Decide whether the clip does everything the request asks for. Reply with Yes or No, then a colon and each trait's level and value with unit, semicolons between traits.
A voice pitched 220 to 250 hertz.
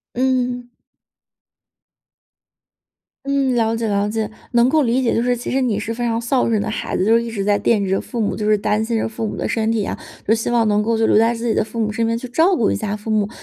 Yes: high, 230 Hz